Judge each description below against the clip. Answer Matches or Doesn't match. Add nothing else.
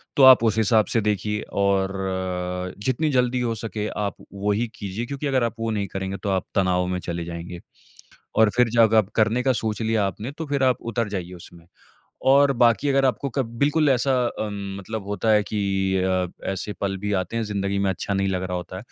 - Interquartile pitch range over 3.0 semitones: Matches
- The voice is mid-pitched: Doesn't match